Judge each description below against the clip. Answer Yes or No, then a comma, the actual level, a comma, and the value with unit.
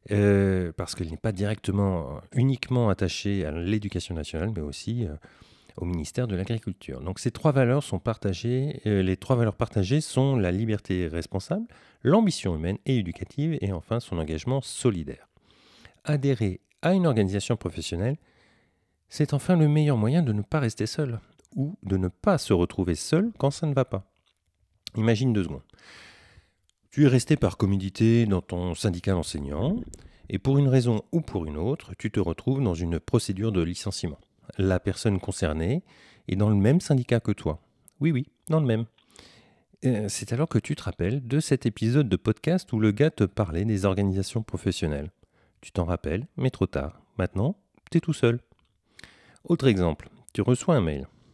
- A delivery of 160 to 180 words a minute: Yes, average, 175 wpm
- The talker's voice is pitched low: Yes, low, 105 Hz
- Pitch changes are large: Yes, wide, 5.8 semitones